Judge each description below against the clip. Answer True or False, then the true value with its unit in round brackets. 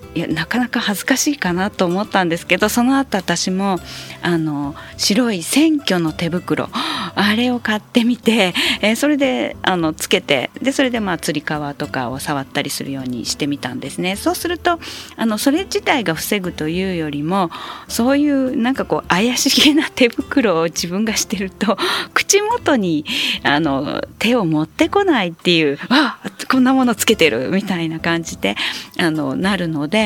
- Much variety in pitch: True (7.7 semitones)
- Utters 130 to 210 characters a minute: False (330 characters per minute)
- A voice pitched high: True (205 Hz)